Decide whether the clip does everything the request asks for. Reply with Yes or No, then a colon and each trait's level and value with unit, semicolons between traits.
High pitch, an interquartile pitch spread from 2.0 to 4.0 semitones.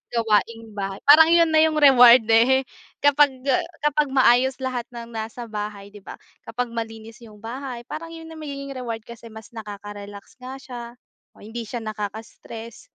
Yes: high, 235 Hz; average, 3.5 semitones